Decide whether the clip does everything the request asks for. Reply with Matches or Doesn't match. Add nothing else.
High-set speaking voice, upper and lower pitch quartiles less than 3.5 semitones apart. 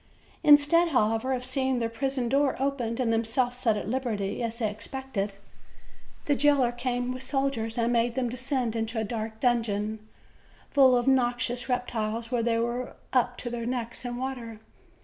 Matches